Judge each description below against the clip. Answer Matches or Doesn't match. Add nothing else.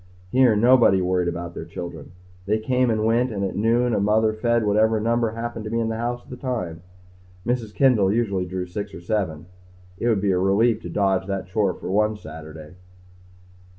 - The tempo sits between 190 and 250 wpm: Matches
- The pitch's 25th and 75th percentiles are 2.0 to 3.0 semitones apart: Doesn't match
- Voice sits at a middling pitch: Doesn't match